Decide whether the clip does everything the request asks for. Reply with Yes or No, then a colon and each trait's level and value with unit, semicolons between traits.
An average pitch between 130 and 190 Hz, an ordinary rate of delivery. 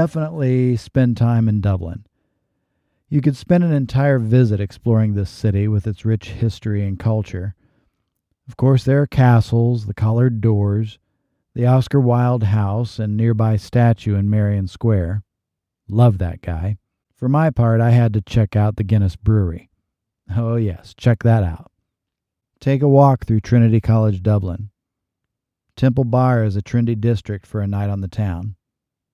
No: low, 110 Hz; average, 155 wpm